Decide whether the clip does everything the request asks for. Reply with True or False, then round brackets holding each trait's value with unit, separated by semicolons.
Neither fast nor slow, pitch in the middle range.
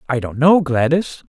True (185 wpm; 145 Hz)